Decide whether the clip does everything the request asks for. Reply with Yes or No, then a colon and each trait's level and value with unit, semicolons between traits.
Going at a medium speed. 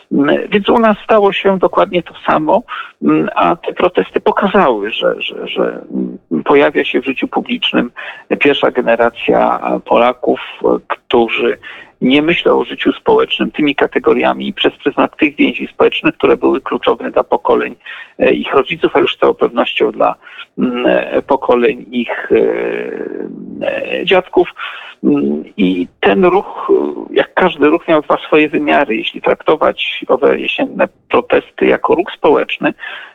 Yes: average, 130 wpm